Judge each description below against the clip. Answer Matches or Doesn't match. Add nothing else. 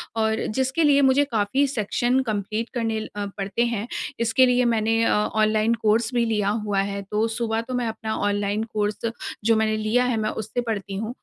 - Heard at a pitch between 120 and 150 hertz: Doesn't match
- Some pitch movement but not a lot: Doesn't match